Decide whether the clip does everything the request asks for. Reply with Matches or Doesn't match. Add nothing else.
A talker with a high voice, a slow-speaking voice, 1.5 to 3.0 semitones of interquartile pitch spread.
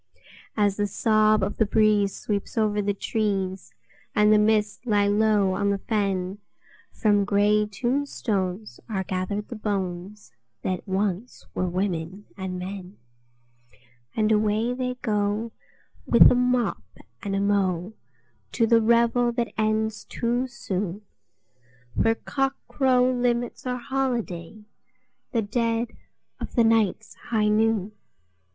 Matches